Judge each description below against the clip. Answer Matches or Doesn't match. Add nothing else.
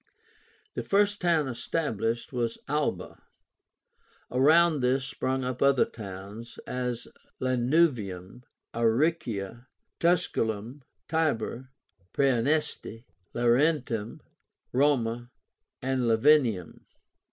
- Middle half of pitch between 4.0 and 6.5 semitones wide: Matches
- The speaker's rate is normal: Doesn't match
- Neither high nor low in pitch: Doesn't match